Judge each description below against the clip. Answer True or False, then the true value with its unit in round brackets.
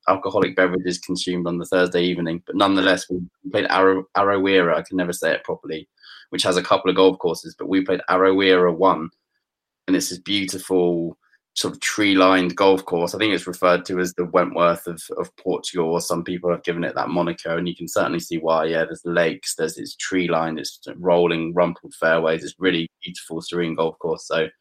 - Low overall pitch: True (90 Hz)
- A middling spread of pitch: False (1.5 semitones)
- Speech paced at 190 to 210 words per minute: True (200 wpm)